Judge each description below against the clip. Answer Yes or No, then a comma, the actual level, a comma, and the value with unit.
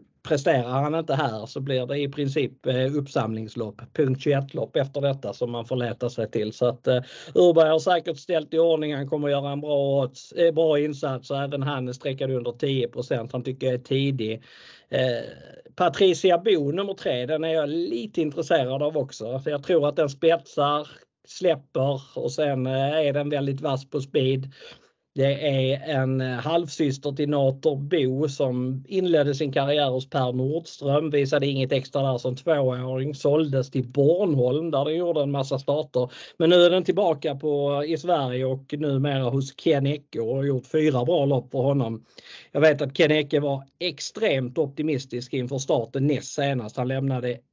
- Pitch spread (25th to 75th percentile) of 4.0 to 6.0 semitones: No, average, 2.8 semitones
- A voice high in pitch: No, medium, 140 Hz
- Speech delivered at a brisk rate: No, average, 175 wpm